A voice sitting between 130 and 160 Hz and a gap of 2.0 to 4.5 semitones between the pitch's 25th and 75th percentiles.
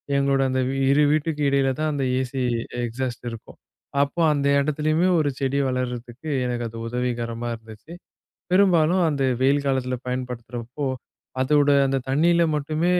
Yes: low, 135 Hz; average, 3.3 semitones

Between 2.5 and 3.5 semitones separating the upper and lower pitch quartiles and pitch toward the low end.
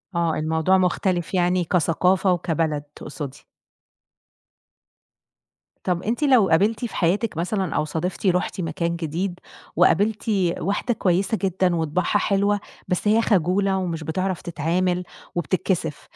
No: average, 2.8 semitones; medium, 180 Hz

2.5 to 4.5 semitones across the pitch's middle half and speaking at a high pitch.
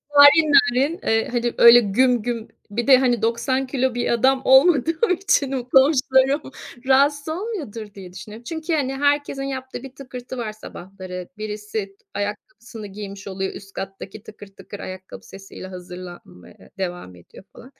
No: average, 5.3 semitones; high, 240 Hz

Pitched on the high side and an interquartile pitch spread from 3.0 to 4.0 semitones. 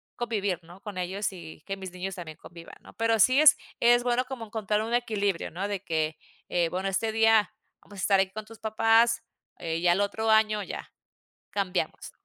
Yes: high, 205 Hz; average, 3.6 semitones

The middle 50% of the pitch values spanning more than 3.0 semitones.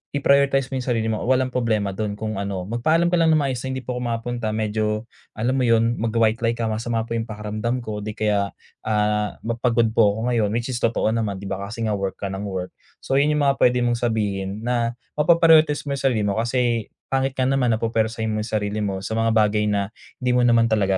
No: average, 2.7 semitones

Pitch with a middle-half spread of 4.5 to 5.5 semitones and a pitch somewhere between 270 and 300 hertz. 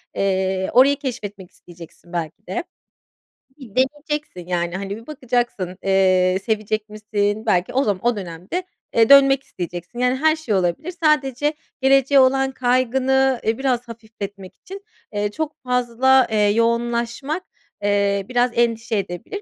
No: average, 5.1 semitones; high, 230 Hz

